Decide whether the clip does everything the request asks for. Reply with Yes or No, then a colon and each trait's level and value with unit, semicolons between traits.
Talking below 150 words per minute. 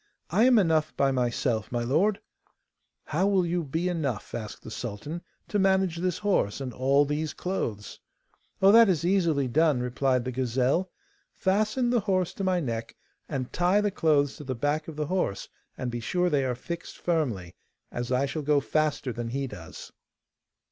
No: average, 180 wpm